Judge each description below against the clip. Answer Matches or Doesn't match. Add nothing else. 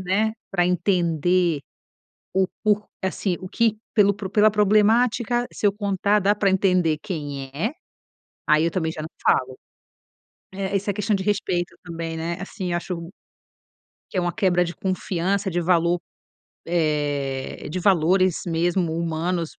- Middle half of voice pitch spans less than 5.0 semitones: Matches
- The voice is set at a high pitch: Doesn't match